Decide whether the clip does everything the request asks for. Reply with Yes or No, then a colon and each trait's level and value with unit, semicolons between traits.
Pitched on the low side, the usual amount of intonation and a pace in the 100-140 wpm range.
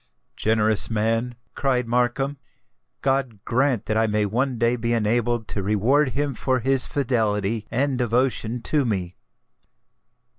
Yes: low, 120 Hz; average, 3.1 semitones; slow, 135 wpm